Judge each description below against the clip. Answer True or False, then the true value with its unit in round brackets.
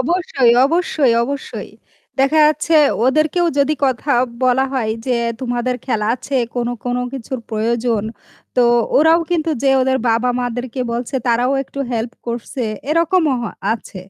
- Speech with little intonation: False (3.9 semitones)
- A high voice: True (260 Hz)